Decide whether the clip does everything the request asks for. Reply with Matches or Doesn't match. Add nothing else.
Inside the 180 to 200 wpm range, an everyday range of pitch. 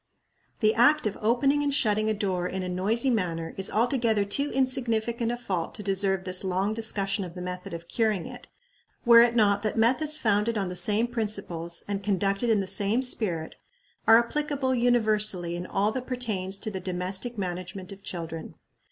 Matches